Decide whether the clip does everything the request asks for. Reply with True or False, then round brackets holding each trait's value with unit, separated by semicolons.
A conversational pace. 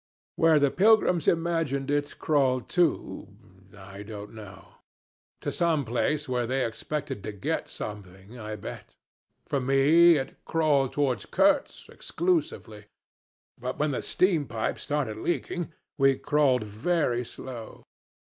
False (130 wpm)